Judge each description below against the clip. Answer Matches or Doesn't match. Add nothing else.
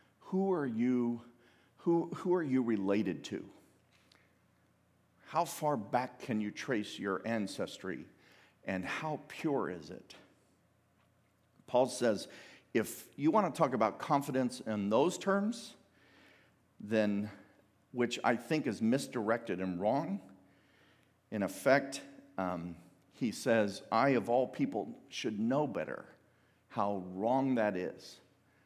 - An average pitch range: Doesn't match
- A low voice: Matches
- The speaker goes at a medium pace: Doesn't match